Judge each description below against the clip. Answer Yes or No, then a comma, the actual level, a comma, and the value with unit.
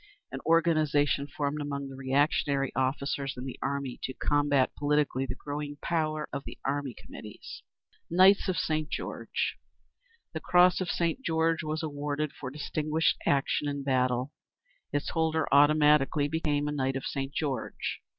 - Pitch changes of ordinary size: No, narrow, 2.1 semitones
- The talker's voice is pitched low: No, medium, 145 Hz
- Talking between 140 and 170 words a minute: Yes, average, 150 wpm